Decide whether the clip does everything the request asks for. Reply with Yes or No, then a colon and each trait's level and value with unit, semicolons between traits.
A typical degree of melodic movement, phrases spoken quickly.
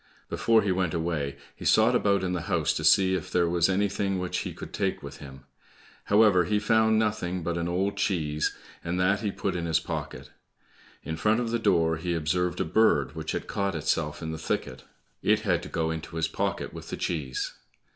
Yes: average, 3.8 semitones; fast, 210 wpm